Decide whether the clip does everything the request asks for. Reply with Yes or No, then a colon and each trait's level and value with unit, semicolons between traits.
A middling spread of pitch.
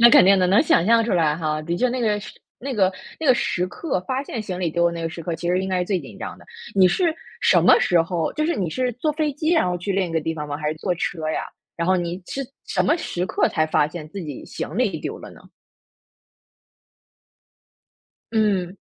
No: wide, 5.7 semitones